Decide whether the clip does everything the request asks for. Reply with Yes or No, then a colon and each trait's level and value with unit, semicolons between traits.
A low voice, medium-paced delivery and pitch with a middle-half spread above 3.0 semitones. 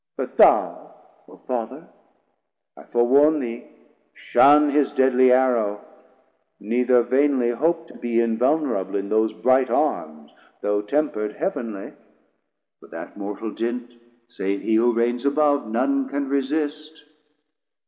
No: low, 125 Hz; slow, 125 wpm; average, 3.9 semitones